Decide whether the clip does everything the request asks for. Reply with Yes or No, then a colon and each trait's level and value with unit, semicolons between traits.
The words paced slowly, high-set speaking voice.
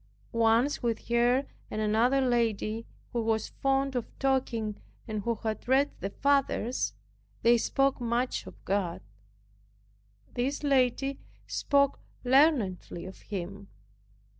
Yes: slow, 115 wpm; high, 240 Hz